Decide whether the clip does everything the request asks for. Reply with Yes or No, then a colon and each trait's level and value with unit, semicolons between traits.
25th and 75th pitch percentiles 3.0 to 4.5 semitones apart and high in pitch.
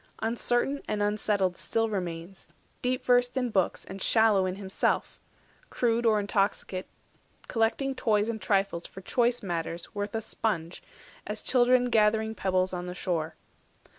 Yes: average, 3.7 semitones; high, 210 Hz